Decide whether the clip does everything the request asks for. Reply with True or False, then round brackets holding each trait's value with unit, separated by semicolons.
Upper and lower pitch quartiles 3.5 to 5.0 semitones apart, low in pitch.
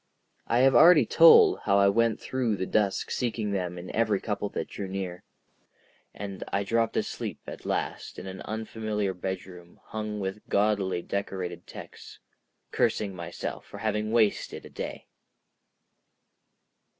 False (2.5 semitones; 100 Hz)